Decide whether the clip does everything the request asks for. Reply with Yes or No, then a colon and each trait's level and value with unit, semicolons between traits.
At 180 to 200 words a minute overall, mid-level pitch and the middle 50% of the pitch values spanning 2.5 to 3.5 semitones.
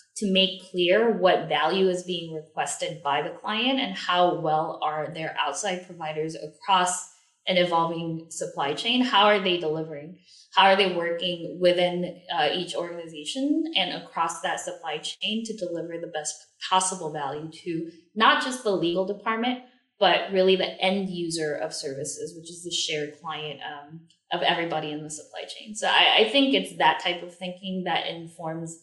No: average, 170 wpm; medium, 175 Hz; average, 2.8 semitones